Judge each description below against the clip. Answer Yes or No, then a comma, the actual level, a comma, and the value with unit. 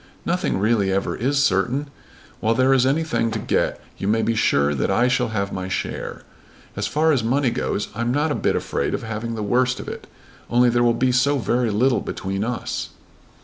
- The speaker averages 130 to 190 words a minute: No, fast, 205 wpm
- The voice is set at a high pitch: No, low, 120 Hz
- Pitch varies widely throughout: No, average, 3.4 semitones